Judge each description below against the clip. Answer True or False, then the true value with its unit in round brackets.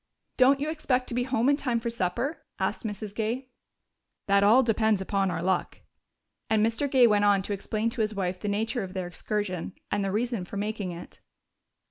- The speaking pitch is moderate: False (215 Hz)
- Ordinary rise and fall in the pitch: True (3.5 semitones)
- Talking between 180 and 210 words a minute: True (200 wpm)